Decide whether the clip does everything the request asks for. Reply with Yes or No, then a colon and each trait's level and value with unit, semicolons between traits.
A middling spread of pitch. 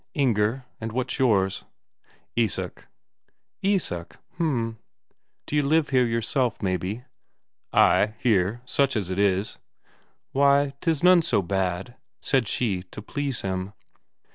No: wide, 5.9 semitones